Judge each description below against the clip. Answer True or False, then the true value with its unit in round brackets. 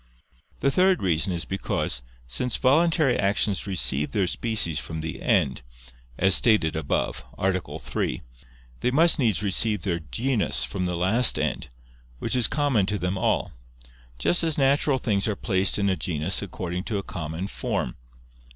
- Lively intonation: True (5.9 semitones)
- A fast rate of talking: False (160 wpm)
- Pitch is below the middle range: True (100 Hz)